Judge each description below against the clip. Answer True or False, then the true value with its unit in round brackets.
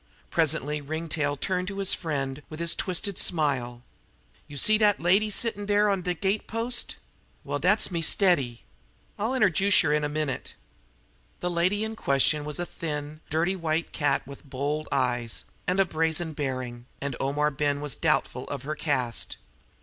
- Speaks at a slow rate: False (165 wpm)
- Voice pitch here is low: False (155 Hz)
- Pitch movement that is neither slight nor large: True (4.8 semitones)